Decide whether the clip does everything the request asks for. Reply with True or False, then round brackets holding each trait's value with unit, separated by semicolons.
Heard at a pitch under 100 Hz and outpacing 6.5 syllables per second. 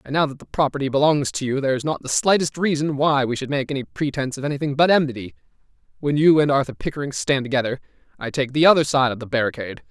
False (140 Hz; 7.0 syllables/s)